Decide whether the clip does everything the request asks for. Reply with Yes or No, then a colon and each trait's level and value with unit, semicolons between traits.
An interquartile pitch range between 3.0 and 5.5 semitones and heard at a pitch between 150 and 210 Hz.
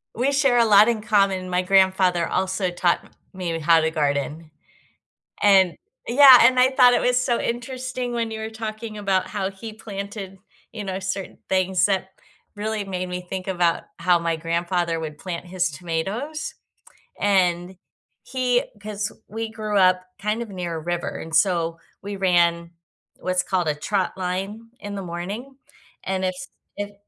Yes: average, 3.6 semitones; high, 190 Hz